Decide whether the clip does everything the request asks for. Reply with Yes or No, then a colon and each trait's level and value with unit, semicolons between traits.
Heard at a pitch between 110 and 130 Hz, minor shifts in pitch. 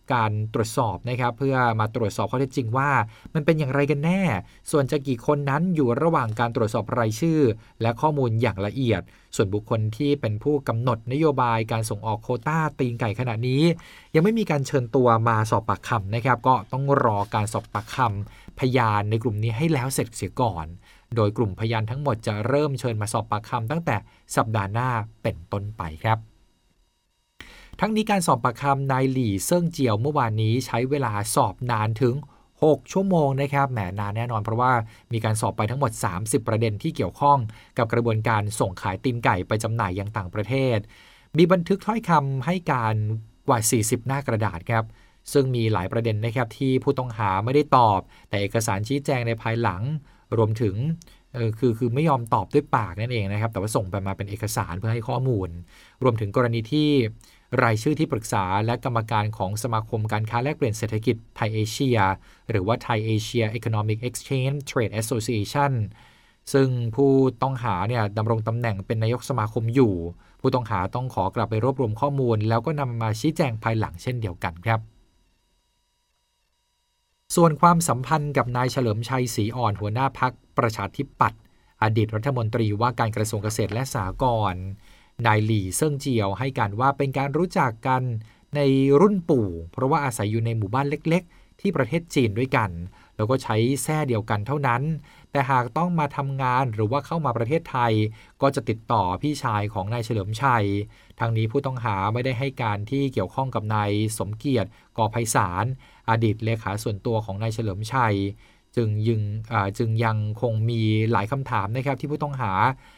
No: low, 115 Hz; average, 3.8 semitones